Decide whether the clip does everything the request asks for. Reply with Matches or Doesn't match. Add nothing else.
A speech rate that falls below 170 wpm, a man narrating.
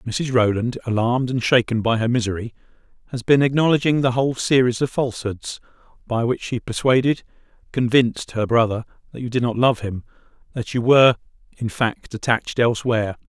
Matches